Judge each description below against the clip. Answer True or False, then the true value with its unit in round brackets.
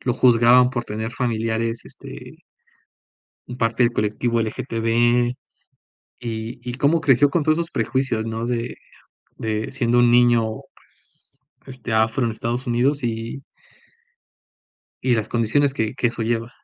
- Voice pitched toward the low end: True (120 Hz)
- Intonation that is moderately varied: False (1.9 semitones)